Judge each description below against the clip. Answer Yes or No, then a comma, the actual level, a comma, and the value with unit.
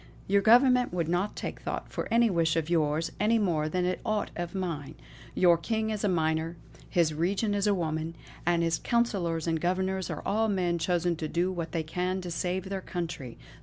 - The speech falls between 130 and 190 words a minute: No, fast, 205 wpm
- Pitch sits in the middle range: Yes, medium, 175 Hz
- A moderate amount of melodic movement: Yes, average, 3.2 semitones